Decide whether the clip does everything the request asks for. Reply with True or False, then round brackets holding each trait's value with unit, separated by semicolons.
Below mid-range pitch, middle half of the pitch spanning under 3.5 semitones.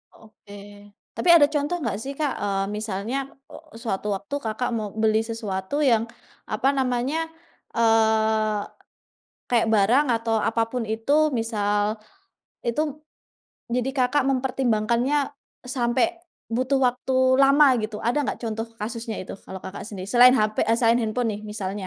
False (230 Hz; 2.8 semitones)